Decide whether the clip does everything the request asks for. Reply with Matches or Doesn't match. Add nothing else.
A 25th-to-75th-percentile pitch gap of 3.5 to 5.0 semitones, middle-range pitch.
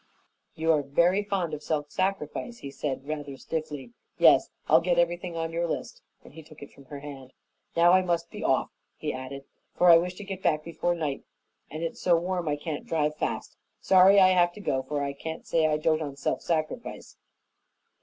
Doesn't match